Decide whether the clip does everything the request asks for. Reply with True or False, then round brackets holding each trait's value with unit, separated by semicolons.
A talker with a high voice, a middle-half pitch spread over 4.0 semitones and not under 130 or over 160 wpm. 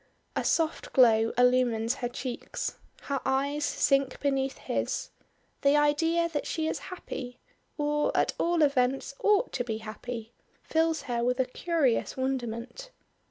False (270 Hz; 3.4 semitones; 140 wpm)